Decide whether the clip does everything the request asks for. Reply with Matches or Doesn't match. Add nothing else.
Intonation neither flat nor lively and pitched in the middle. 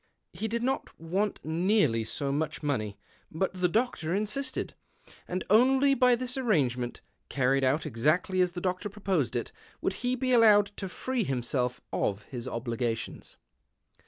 Doesn't match